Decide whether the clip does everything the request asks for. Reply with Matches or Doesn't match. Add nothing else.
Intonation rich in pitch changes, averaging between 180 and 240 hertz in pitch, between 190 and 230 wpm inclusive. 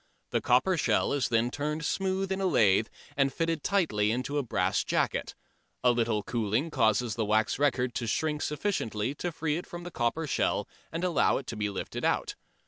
Doesn't match